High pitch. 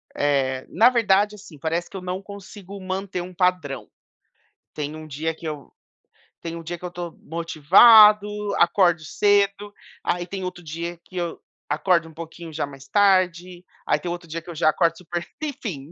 No: medium, 175 Hz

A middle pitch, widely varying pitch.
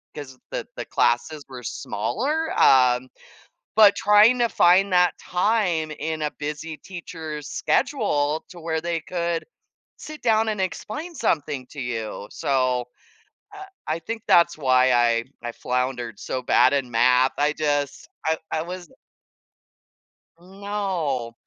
Yes: medium, 155 Hz; wide, 6.6 semitones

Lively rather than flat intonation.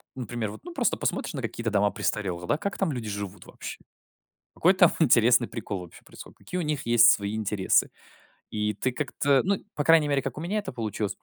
Yes: wide, 6.3 semitones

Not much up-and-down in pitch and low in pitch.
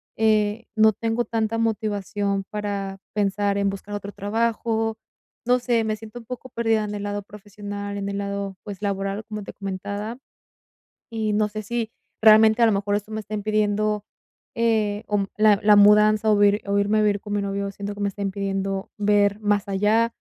No: narrow, 1.4 semitones; high, 210 Hz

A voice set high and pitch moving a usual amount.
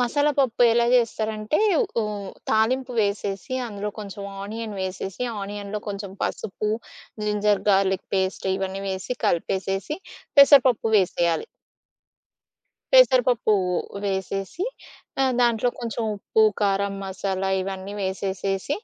Yes: high, 205 Hz; average, 3.4 semitones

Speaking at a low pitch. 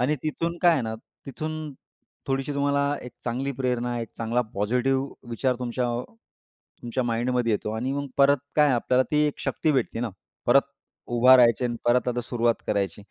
Yes: low, 125 Hz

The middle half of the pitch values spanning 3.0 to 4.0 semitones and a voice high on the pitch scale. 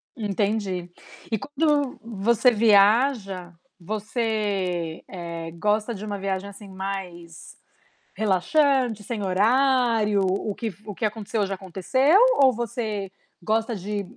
Yes: average, 3.3 semitones; high, 210 Hz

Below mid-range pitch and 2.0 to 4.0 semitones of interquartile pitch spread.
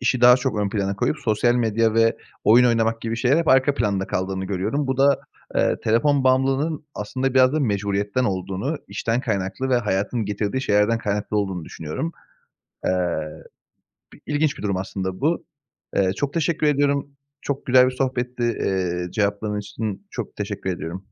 No: low, 115 Hz; average, 4.8 semitones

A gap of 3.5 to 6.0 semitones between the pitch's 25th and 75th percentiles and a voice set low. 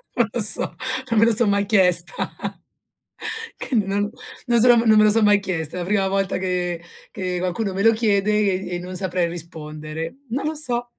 No: average, 3.9 semitones; high, 200 Hz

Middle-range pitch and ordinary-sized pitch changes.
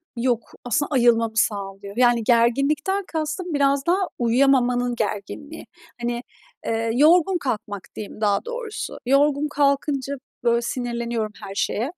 No: high, 245 Hz; average, 4.1 semitones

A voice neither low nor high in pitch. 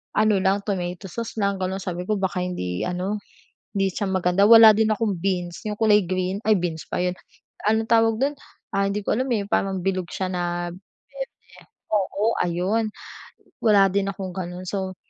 No: high, 195 Hz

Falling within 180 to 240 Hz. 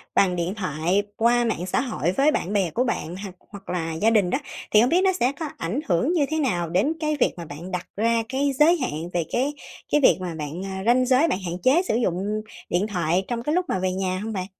Yes: high, 205 Hz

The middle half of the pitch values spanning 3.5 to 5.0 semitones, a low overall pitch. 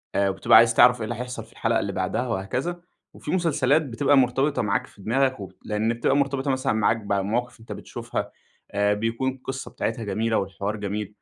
Yes: average, 4.1 semitones; low, 115 Hz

